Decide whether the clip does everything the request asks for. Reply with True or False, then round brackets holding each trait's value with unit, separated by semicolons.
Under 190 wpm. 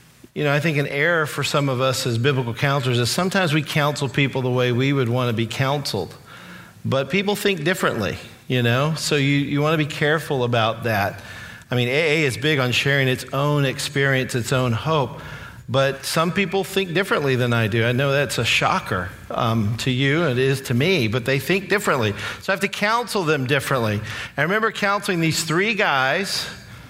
False (205 wpm)